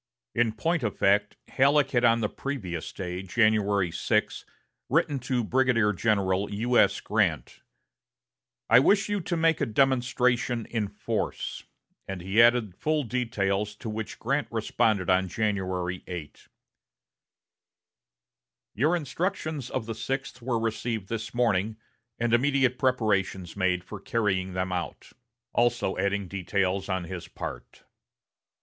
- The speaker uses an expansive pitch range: No, average, 4.5 semitones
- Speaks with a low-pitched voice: Yes, low, 110 Hz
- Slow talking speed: Yes, slow, 130 wpm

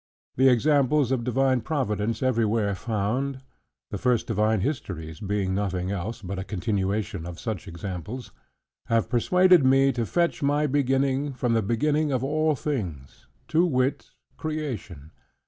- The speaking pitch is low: Yes, low, 120 Hz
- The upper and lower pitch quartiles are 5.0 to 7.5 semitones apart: Yes, wide, 5.4 semitones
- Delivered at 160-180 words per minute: No, average, 140 wpm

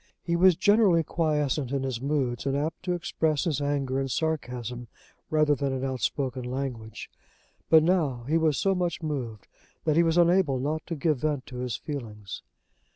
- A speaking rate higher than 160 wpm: Yes, average, 175 wpm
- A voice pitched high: No, medium, 145 Hz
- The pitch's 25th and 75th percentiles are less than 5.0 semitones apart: Yes, average, 3.8 semitones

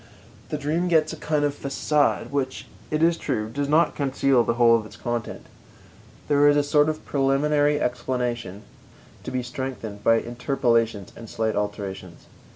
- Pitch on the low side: Yes, low, 130 Hz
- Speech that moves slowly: No, average, 160 wpm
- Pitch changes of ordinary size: Yes, average, 4.1 semitones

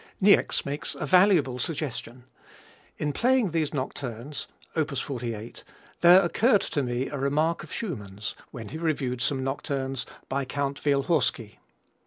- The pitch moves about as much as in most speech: Yes, average, 4.2 semitones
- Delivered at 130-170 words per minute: Yes, slow, 135 wpm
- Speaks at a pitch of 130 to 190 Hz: Yes, medium, 140 Hz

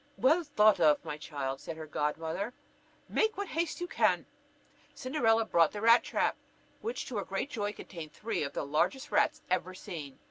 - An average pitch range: No, wide, 8.6 semitones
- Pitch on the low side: No, high, 205 Hz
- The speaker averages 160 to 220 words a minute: Yes, average, 180 wpm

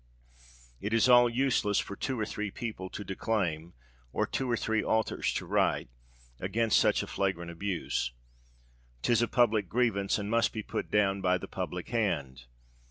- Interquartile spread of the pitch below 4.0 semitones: Yes, average, 3.6 semitones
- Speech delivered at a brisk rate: No, average, 165 wpm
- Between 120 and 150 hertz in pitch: No, low, 105 Hz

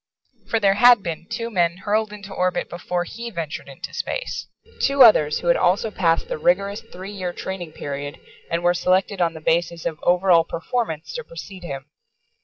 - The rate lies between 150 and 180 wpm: No, average, 190 wpm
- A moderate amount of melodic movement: Yes, average, 3.6 semitones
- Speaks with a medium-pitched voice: Yes, medium, 180 Hz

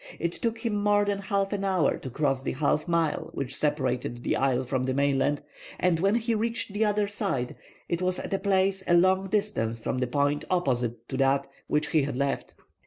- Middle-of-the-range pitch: Yes, medium, 160 Hz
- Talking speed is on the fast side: Yes, fast, 210 wpm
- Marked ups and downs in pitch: Yes, wide, 6.6 semitones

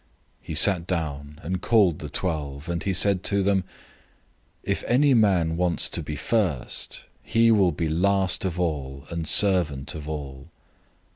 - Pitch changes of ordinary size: Yes, average, 4.5 semitones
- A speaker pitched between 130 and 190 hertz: No, very low, 85 Hz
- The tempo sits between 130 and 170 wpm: Yes, average, 160 wpm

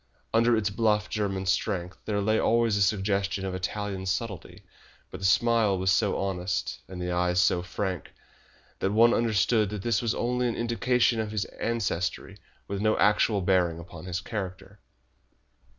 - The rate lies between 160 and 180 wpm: Yes, average, 165 wpm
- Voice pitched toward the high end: No, low, 100 Hz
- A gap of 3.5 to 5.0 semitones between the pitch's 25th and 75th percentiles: No, average, 3.1 semitones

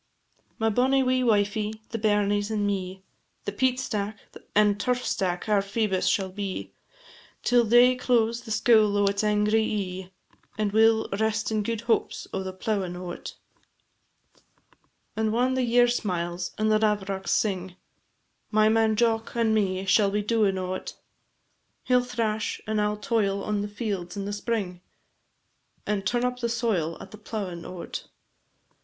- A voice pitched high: Yes, high, 210 Hz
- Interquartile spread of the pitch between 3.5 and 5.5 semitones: No, narrow, 2.4 semitones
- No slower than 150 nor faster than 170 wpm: Yes, average, 160 wpm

